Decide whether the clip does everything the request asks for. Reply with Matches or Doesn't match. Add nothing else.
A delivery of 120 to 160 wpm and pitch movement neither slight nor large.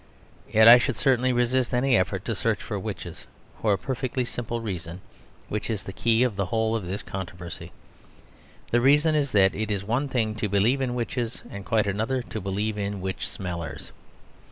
Doesn't match